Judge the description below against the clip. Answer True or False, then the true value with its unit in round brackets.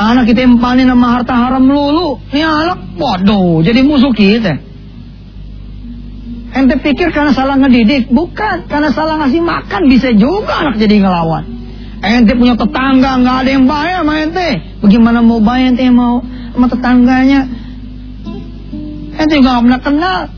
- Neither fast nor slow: True (150 wpm)